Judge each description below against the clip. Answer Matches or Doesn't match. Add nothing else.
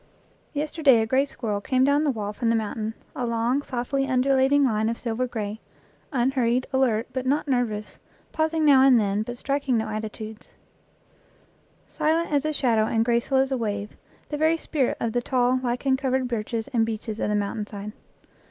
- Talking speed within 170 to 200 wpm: Matches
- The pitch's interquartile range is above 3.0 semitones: Matches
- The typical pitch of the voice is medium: Doesn't match